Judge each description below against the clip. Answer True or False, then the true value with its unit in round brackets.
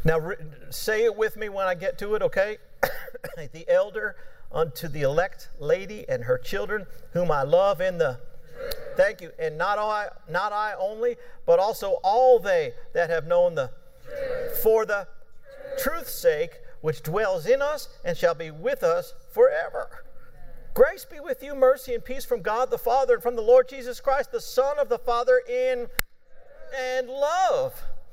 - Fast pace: False (170 wpm)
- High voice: True (270 Hz)